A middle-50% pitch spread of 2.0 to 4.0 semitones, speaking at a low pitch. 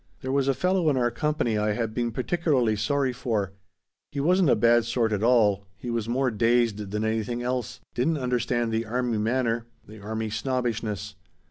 Yes: average, 2.8 semitones; low, 120 Hz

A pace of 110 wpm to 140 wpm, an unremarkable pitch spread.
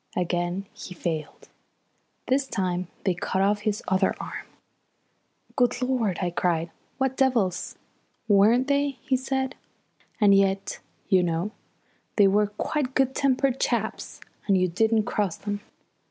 No: slow, 135 wpm; wide, 5.8 semitones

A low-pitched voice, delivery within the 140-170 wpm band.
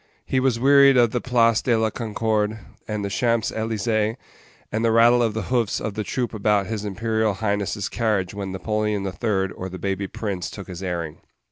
No: low, 110 Hz; average, 200 wpm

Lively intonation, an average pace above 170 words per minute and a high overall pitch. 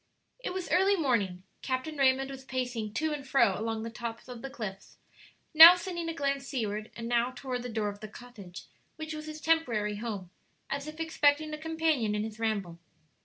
Yes: wide, 5.9 semitones; average, 195 wpm; very high, 255 Hz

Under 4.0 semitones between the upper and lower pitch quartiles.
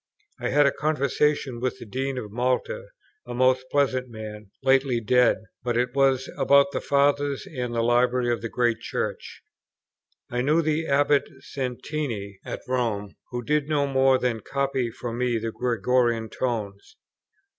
Yes: average, 2.9 semitones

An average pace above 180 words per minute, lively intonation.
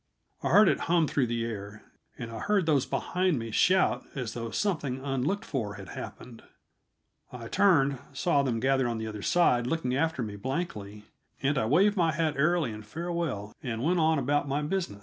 Yes: average, 190 wpm; wide, 6.2 semitones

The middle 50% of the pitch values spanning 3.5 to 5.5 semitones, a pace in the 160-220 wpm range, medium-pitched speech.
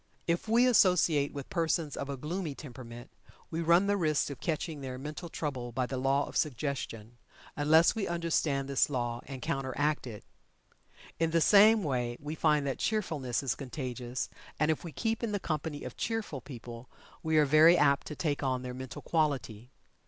Yes: average, 4.1 semitones; average, 180 wpm; medium, 145 Hz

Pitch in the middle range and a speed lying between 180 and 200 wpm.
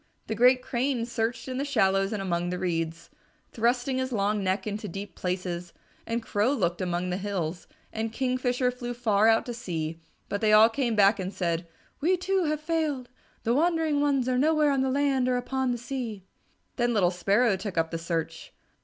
No: high, 225 Hz; average, 195 wpm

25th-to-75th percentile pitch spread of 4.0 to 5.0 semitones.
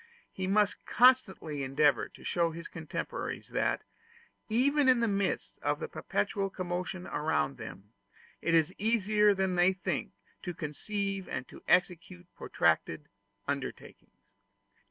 Yes: average, 4.3 semitones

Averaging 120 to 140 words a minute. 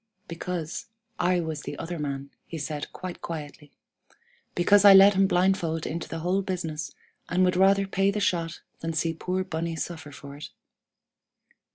No: average, 165 wpm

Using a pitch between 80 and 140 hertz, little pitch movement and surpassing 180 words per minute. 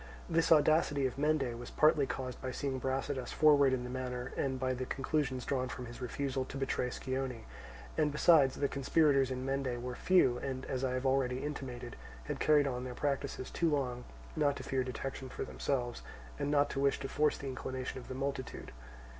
Yes: low, 135 Hz; narrow, 1.9 semitones; average, 195 wpm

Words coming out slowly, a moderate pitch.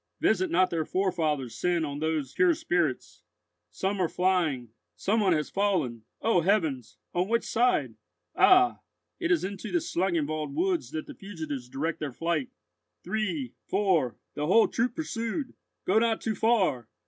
No: average, 150 wpm; medium, 180 Hz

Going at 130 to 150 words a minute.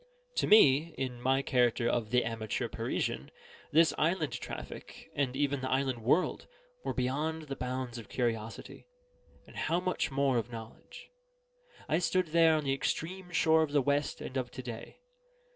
No: average, 165 wpm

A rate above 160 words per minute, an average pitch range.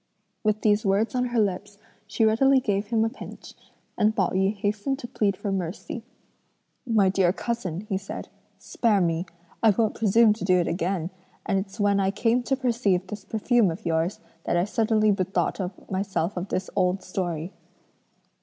Yes: average, 175 wpm; average, 3.0 semitones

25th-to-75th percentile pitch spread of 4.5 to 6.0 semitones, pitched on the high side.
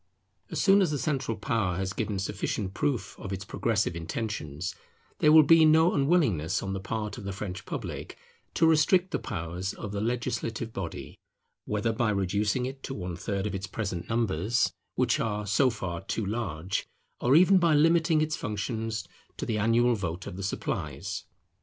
No: wide, 5.5 semitones; low, 105 Hz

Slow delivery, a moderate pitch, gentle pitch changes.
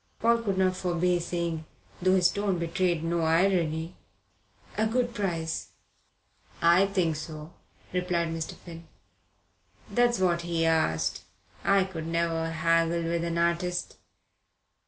Yes: slow, 125 wpm; medium, 170 Hz; narrow, 2.2 semitones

